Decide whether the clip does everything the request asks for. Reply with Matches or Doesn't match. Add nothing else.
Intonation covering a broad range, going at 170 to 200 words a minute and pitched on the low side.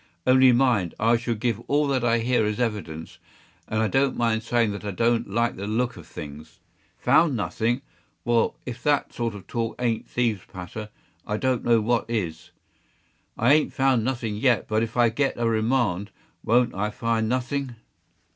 Doesn't match